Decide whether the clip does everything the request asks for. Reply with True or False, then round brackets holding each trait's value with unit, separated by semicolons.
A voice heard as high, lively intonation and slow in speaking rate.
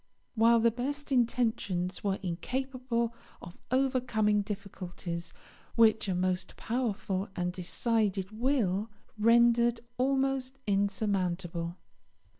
False (220 Hz; 4.4 semitones; 90 wpm)